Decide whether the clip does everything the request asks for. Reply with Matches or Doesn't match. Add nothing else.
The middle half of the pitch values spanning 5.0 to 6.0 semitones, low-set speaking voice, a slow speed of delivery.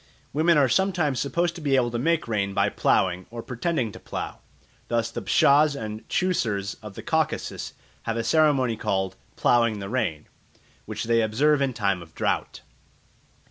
Doesn't match